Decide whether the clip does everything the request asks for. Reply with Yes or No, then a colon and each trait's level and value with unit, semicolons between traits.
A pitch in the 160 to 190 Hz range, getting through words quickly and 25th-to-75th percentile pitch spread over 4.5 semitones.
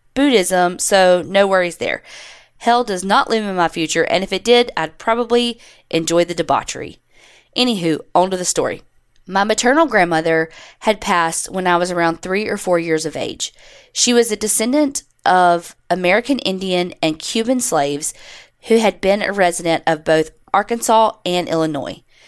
No: medium, 185 Hz; average, 165 wpm; average, 4.9 semitones